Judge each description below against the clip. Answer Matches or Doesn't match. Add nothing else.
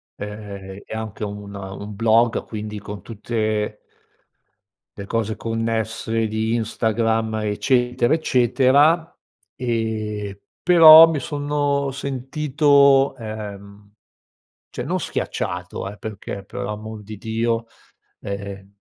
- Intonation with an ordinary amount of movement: Matches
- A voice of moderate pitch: Doesn't match